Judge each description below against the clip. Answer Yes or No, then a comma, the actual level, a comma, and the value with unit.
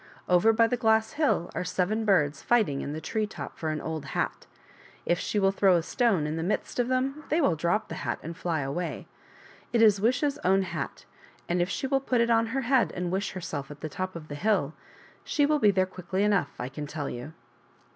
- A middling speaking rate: No, fast, 230 wpm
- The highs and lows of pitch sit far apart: Yes, wide, 5.9 semitones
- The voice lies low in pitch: No, high, 190 Hz